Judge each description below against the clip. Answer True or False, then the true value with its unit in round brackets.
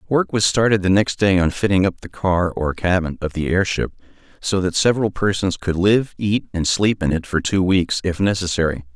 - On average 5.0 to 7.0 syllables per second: True (5.2 syllables/s)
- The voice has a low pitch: True (95 Hz)